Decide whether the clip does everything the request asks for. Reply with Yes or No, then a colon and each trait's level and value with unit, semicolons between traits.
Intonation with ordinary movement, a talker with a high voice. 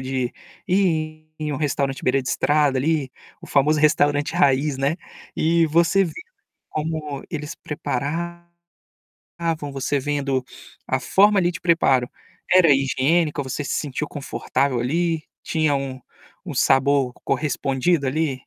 No: average, 3.2 semitones; medium, 145 Hz